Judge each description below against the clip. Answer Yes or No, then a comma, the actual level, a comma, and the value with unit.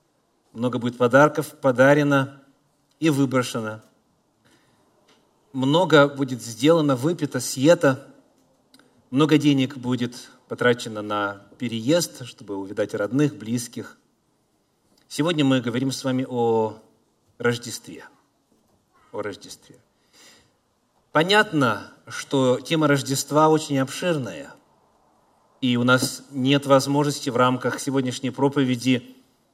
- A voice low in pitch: Yes, low, 130 Hz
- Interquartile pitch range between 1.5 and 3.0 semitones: Yes, narrow, 2.6 semitones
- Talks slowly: Yes, slow, 90 wpm